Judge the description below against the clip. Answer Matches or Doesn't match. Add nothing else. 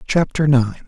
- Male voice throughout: Matches